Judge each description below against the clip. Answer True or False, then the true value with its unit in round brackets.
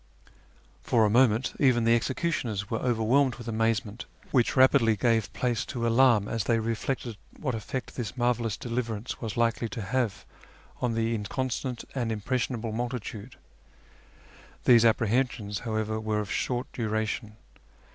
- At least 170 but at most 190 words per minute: False (135 wpm)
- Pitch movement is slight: True (2.2 semitones)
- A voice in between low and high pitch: False (115 Hz)